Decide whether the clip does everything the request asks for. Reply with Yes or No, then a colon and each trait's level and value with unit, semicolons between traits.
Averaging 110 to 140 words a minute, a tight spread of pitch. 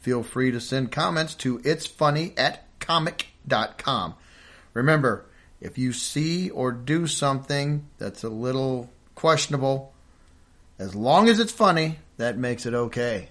No: slow, 135 wpm; average, 4.4 semitones